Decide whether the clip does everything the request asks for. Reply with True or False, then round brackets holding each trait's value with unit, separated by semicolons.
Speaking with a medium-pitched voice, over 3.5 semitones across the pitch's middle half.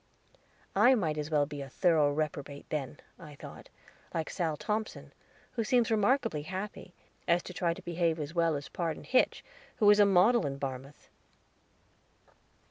True (165 Hz; 5.6 semitones)